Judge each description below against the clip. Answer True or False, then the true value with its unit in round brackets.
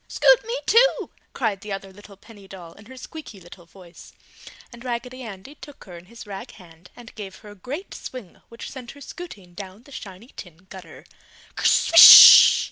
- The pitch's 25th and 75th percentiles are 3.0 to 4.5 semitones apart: False (5.3 semitones)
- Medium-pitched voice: False (205 Hz)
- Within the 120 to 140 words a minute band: False (185 wpm)